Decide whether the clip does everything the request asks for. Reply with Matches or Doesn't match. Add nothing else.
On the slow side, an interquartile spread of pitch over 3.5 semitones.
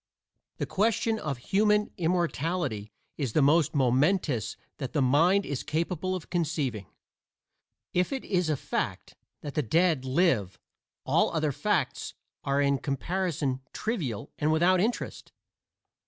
Matches